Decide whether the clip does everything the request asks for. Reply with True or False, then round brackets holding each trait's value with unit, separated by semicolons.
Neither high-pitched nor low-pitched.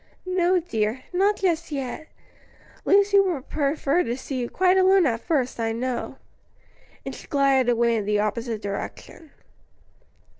False (275 Hz)